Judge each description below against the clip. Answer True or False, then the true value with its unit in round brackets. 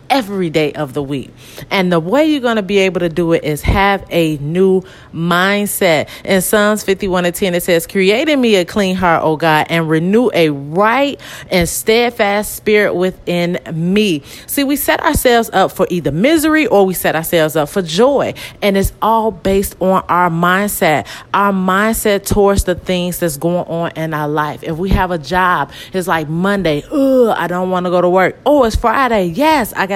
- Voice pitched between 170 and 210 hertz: True (185 Hz)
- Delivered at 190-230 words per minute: True (200 wpm)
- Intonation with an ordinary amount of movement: True (3.8 semitones)